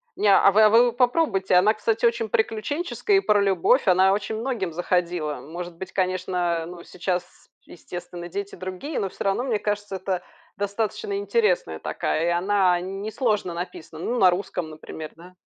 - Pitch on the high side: Yes, high, 195 Hz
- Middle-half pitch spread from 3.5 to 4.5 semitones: Yes, average, 3.8 semitones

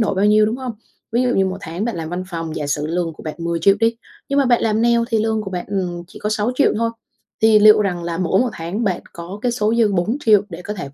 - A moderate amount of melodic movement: Yes, average, 4.5 semitones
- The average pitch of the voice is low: No, high, 205 Hz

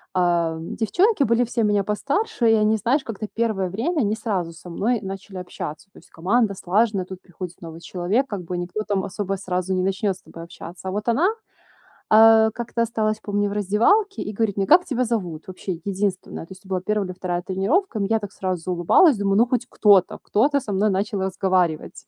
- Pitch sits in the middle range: No, high, 200 Hz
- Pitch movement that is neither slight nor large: Yes, average, 3.3 semitones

